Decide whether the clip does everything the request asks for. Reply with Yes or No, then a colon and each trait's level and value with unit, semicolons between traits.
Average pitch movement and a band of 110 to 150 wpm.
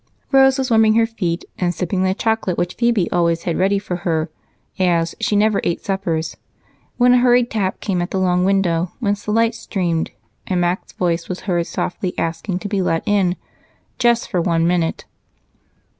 No: average, 3.9 semitones; average, 185 wpm